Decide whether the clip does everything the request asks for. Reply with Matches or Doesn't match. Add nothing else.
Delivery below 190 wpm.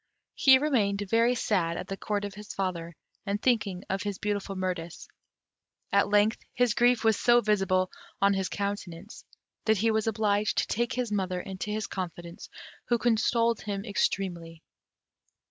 Matches